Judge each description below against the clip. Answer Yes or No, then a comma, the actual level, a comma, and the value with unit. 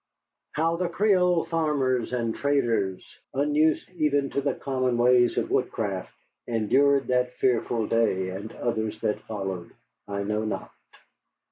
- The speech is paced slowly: Yes, slow, 130 wpm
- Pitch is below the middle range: Yes, low, 125 Hz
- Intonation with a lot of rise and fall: No, average, 4.8 semitones